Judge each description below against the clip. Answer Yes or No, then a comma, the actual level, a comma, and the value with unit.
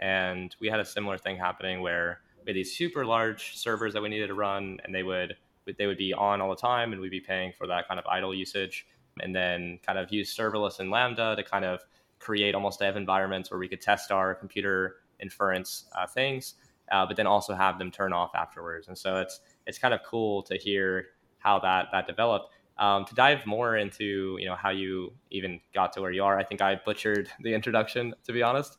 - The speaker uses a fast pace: Yes, fast, 225 wpm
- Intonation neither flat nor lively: No, narrow, 2.2 semitones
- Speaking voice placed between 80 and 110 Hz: Yes, low, 100 Hz